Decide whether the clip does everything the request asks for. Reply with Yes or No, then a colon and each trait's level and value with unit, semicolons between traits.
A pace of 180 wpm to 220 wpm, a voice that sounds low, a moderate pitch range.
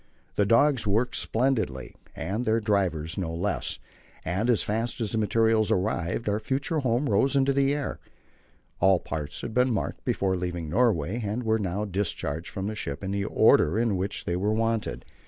Yes: average, 185 wpm; low, 105 Hz; average, 3.8 semitones